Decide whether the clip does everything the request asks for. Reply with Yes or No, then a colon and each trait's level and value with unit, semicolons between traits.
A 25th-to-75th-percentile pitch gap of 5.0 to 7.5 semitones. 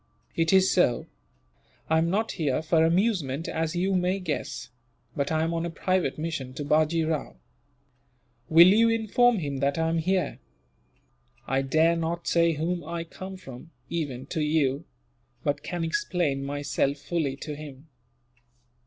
No: average, 3.4 semitones